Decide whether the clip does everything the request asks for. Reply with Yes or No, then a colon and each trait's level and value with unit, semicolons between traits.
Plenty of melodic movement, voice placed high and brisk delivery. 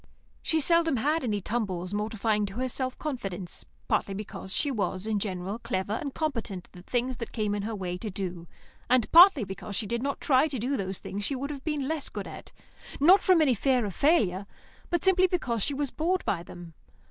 Yes: wide, 6.4 semitones; high, 230 Hz; fast, 210 wpm